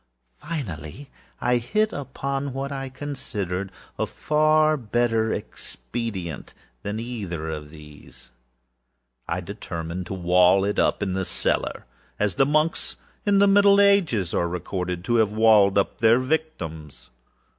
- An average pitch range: No, wide, 7.5 semitones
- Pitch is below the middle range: Yes, low, 110 Hz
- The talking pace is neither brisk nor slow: No, slow, 130 wpm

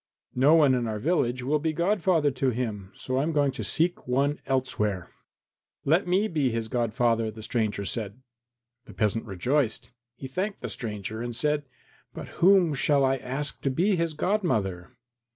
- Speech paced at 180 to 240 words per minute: No, average, 170 wpm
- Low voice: Yes, low, 130 Hz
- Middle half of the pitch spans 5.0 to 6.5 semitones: Yes, average, 5.3 semitones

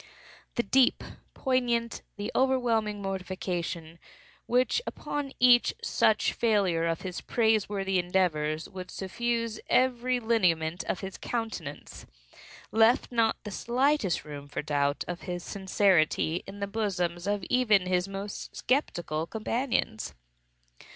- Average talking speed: No, slow, 125 wpm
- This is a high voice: Yes, high, 200 Hz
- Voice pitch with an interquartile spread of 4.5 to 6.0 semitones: Yes, average, 5.0 semitones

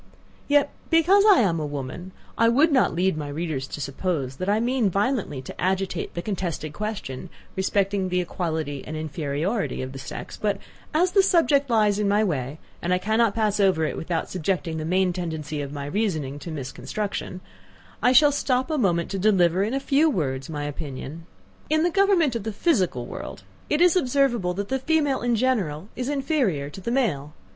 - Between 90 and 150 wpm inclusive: No, average, 190 wpm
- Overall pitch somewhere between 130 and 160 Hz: No, high, 190 Hz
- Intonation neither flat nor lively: No, wide, 8.0 semitones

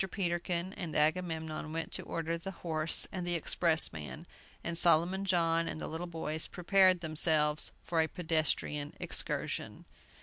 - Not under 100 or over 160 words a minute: Yes, average, 140 wpm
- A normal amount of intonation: No, narrow, 1.9 semitones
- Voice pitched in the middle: Yes, medium, 165 Hz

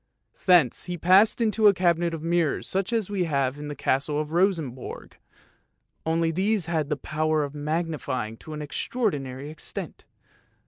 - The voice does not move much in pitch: No, average, 3.7 semitones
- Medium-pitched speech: Yes, medium, 160 Hz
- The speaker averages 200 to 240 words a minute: No, average, 165 wpm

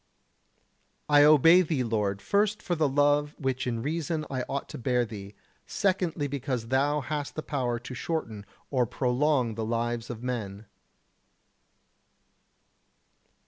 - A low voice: Yes, low, 130 Hz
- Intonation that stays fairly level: No, average, 4.2 semitones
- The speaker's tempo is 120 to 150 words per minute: Yes, slow, 135 wpm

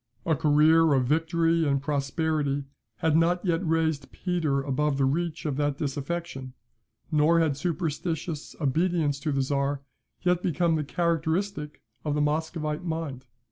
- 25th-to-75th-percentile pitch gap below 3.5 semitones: Yes, average, 2.7 semitones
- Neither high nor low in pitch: Yes, medium, 155 Hz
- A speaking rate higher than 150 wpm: No, average, 140 wpm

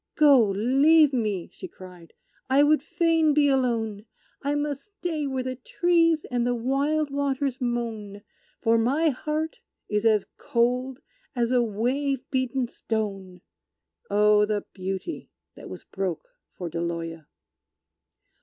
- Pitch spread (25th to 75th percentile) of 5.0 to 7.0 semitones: Yes, wide, 5.5 semitones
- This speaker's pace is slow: Yes, slow, 130 wpm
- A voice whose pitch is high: Yes, very high, 250 Hz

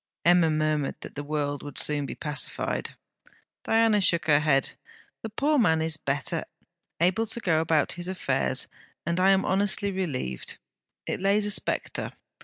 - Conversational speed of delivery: Yes, average, 160 wpm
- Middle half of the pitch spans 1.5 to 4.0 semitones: No, average, 4.7 semitones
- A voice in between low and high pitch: Yes, medium, 170 Hz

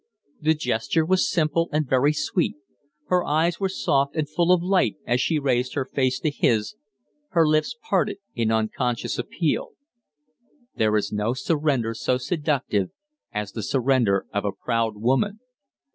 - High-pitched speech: No, low, 135 Hz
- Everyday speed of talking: Yes, average, 155 wpm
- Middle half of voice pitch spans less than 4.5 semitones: No, wide, 5.6 semitones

